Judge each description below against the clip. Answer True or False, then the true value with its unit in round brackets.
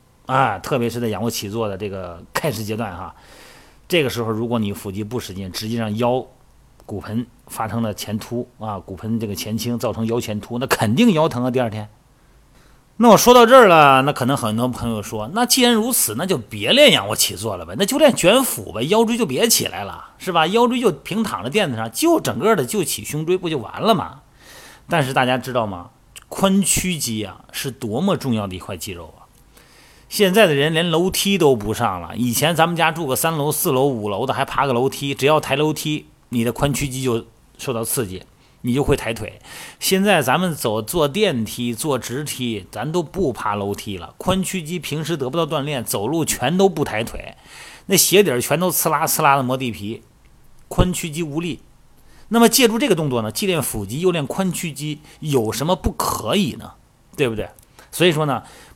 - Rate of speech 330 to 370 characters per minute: False (290 characters per minute)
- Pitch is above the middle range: False (135 Hz)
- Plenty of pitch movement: True (7.2 semitones)